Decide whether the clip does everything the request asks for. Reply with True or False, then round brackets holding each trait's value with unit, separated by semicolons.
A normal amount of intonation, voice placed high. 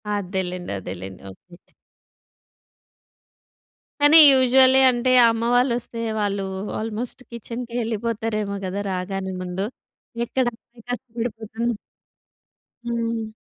True (3.5 semitones; 225 Hz)